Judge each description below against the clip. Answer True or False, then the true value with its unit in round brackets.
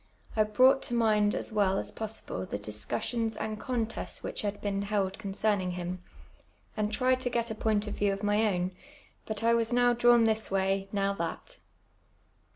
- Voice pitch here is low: False (210 Hz)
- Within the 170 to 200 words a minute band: True (185 wpm)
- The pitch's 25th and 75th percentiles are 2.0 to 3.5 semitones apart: True (2.6 semitones)